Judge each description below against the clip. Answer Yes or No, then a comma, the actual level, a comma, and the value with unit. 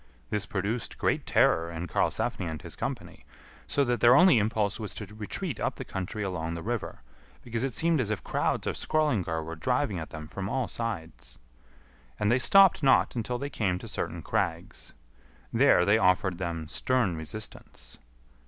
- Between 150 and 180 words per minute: Yes, average, 175 wpm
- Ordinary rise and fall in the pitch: No, wide, 6.2 semitones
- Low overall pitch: Yes, low, 105 Hz